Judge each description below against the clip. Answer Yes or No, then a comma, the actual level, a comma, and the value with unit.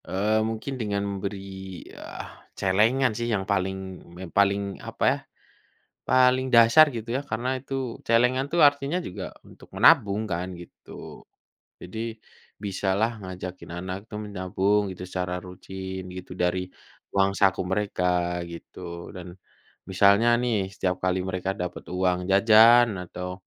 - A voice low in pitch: Yes, low, 100 Hz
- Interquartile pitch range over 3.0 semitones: Yes, average, 3.7 semitones